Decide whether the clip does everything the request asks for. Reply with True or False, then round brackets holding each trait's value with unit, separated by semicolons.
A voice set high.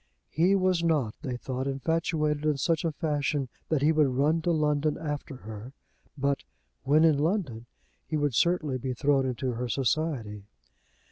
False (145 Hz)